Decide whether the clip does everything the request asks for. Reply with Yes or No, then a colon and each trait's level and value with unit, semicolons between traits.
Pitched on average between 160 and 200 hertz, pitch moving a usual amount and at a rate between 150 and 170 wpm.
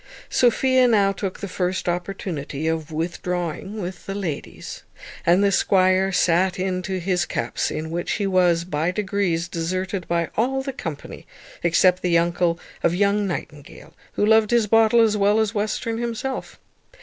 Yes: medium, 185 Hz; average, 3.3 semitones; average, 160 wpm